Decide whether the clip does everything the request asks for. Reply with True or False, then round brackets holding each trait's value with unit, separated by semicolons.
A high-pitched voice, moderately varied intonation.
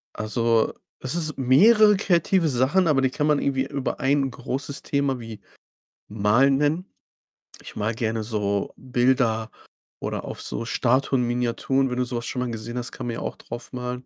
False (125 Hz; 3.0 semitones)